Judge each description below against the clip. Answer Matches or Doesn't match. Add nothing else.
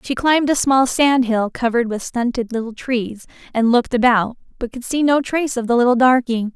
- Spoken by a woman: Matches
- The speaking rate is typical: Doesn't match